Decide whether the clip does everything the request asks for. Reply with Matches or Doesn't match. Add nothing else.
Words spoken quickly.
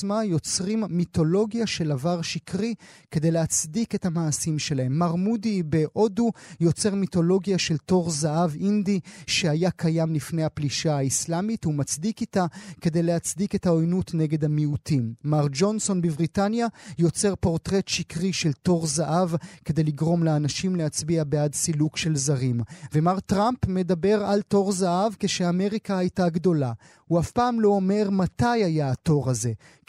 Doesn't match